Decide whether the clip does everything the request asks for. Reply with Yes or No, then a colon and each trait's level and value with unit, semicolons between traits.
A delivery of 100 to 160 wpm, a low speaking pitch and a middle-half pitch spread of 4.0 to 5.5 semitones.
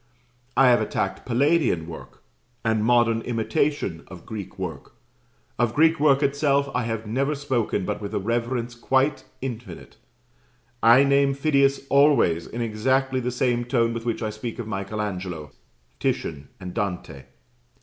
Yes: average, 150 wpm; low, 120 Hz; average, 4.3 semitones